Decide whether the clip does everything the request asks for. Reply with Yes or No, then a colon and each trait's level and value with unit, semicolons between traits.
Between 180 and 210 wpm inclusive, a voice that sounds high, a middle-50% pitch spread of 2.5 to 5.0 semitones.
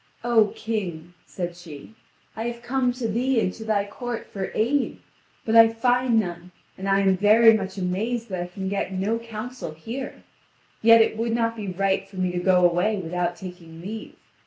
Yes: average, 190 wpm; high, 205 Hz; average, 4.0 semitones